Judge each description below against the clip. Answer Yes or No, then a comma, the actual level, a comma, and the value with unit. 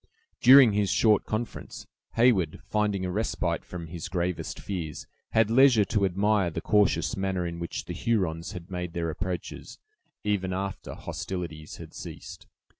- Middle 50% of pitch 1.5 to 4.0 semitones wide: Yes, average, 3.3 semitones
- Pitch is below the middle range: Yes, very low, 95 Hz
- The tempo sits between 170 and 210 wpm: No, average, 150 wpm